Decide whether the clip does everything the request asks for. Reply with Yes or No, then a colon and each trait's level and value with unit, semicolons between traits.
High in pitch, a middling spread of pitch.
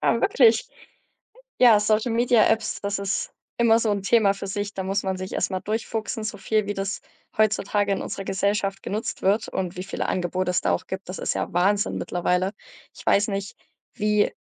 No: high, 200 Hz; narrow, 2.1 semitones